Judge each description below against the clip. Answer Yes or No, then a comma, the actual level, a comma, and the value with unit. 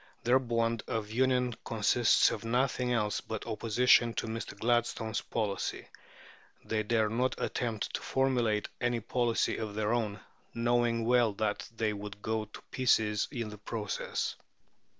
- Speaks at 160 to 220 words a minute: No, average, 145 wpm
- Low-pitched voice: Yes, low, 115 Hz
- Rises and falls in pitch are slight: Yes, narrow, 2.0 semitones